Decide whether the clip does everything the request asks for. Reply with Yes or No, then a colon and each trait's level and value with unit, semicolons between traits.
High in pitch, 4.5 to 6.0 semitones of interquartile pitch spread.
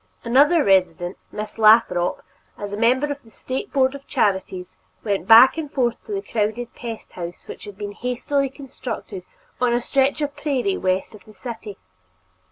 Yes: high, 235 Hz; average, 5.0 semitones